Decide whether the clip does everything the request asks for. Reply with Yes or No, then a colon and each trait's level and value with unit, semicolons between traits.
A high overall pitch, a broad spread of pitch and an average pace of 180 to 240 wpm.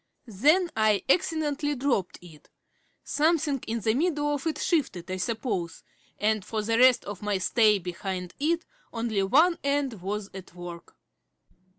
No: high, 225 Hz; wide, 7.2 semitones; average, 150 wpm